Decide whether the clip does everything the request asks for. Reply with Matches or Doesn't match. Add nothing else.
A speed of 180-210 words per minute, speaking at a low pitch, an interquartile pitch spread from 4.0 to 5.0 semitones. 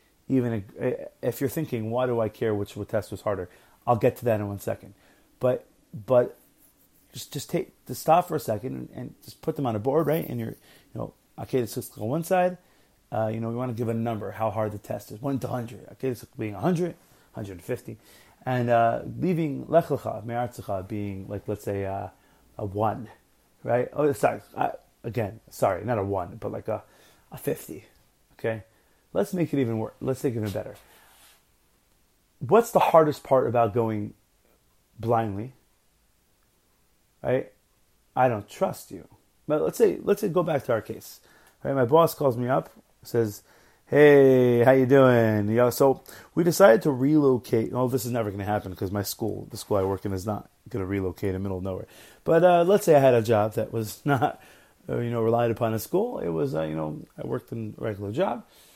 Matches